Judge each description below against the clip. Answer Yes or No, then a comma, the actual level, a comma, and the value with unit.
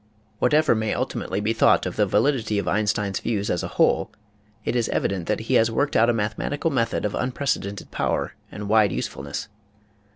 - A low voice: Yes, low, 110 Hz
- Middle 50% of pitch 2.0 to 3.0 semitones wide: Yes, narrow, 2.5 semitones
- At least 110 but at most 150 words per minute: No, average, 185 wpm